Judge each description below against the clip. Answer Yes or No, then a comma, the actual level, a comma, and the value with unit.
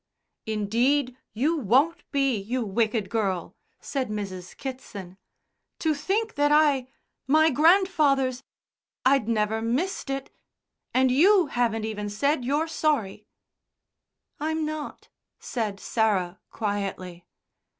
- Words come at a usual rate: No, slow, 110 wpm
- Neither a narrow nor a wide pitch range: No, wide, 5.8 semitones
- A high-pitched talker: Yes, very high, 255 Hz